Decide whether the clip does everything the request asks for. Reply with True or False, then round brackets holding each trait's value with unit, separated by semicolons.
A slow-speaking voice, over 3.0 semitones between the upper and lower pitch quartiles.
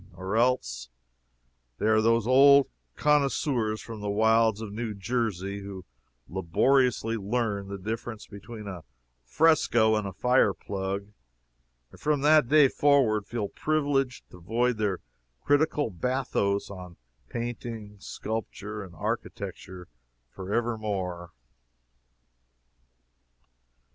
True (110 wpm; 4.0 semitones)